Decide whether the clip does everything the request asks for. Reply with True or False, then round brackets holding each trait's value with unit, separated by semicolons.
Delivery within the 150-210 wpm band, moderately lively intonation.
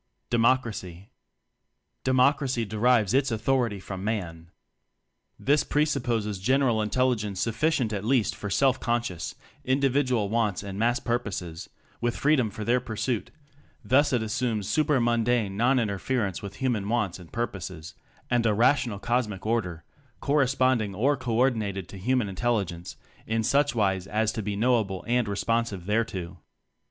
False (140 wpm; 4.1 semitones)